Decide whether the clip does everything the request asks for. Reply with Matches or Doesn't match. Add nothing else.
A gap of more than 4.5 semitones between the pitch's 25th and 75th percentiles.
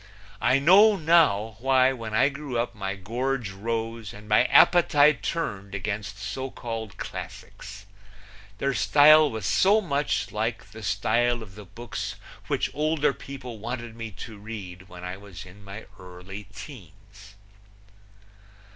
Matches